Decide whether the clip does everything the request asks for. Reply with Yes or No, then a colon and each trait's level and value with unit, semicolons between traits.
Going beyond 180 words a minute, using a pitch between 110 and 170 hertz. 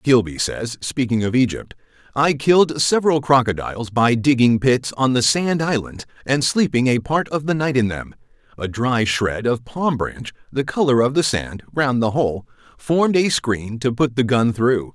Yes: average, 190 wpm; low, 130 Hz